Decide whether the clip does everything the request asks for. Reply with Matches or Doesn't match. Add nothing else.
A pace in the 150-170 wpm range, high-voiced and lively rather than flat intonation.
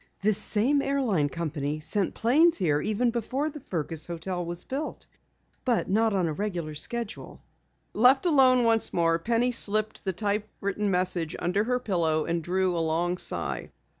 Matches